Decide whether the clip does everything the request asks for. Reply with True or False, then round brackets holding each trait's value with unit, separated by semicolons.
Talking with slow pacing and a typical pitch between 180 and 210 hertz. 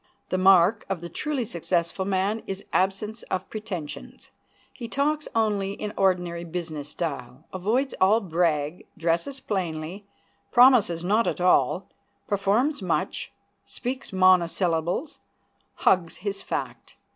True (120 wpm; 190 Hz)